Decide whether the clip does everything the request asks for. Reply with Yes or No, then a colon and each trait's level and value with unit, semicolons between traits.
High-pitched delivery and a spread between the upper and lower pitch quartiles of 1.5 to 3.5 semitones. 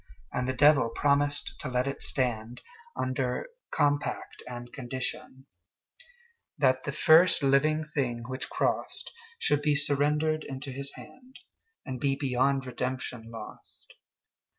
No: medium, 140 Hz; average, 3.1 semitones